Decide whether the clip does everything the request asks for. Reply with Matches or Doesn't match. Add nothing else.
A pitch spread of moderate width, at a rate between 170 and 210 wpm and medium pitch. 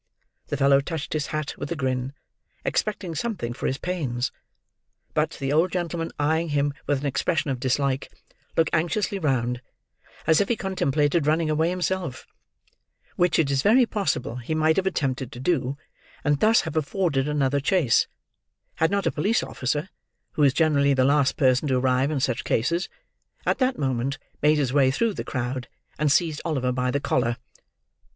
Matches